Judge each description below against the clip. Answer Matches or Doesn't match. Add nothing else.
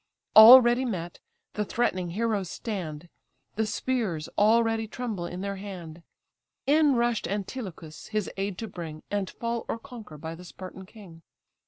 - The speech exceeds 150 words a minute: Doesn't match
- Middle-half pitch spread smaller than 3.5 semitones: Doesn't match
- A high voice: Matches